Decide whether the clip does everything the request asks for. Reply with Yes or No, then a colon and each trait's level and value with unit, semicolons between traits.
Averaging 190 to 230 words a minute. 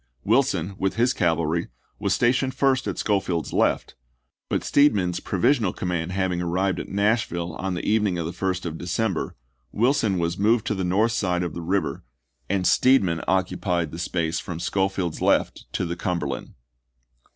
No: average, 170 wpm